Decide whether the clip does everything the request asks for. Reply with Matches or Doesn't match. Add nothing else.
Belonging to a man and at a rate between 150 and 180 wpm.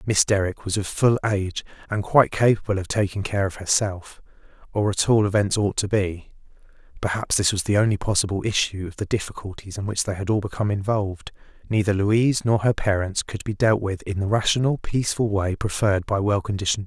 Doesn't match